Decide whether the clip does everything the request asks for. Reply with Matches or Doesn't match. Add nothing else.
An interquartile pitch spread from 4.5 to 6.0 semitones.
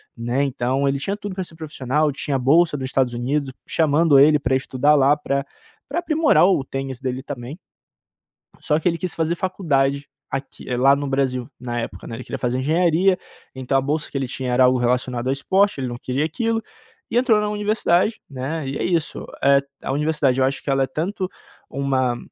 Doesn't match